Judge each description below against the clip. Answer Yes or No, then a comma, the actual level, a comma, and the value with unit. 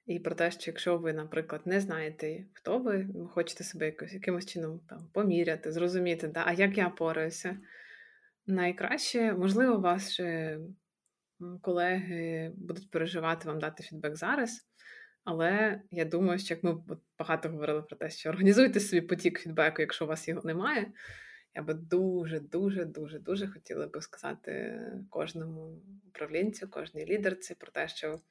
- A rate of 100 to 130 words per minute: No, average, 150 wpm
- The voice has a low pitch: No, medium, 175 Hz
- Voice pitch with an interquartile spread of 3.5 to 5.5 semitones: No, average, 3.0 semitones